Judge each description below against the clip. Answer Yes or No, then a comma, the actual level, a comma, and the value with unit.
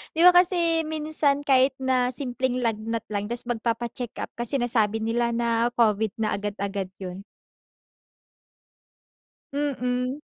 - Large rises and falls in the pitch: No, average, 3.7 semitones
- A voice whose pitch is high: Yes, high, 240 Hz